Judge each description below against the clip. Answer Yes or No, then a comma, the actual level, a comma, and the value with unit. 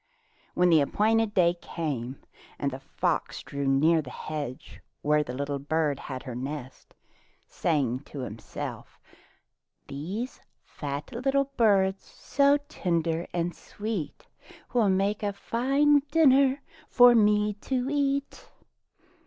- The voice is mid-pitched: Yes, medium, 175 Hz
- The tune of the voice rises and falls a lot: Yes, wide, 8.8 semitones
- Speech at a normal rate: No, slow, 120 wpm